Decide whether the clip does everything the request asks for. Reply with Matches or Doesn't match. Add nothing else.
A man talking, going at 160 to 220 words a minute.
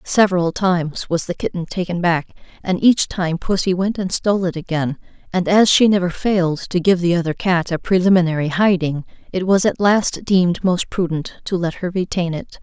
Doesn't match